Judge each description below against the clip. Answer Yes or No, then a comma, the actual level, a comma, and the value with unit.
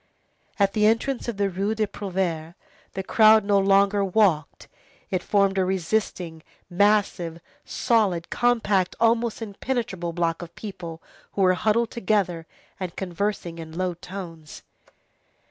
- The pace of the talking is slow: Yes, slow, 130 wpm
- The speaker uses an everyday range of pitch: Yes, average, 3.5 semitones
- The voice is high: Yes, high, 195 Hz